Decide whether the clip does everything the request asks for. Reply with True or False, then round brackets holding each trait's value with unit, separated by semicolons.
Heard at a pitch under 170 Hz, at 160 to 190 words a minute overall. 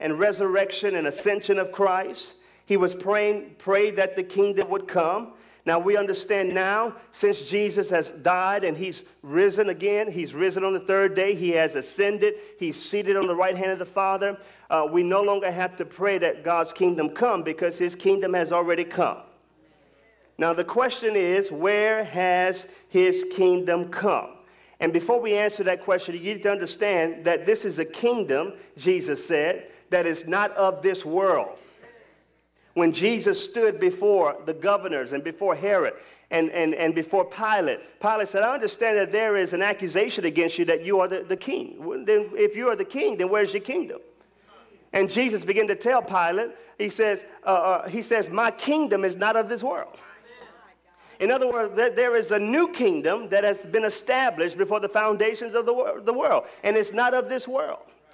False (200 Hz; 185 wpm)